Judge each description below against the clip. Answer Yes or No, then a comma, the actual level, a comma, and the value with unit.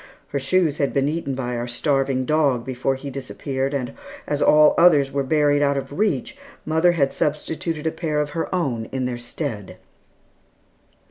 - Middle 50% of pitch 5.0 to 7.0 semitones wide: No, narrow, 2.6 semitones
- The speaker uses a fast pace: No, average, 175 wpm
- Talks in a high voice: No, medium, 140 Hz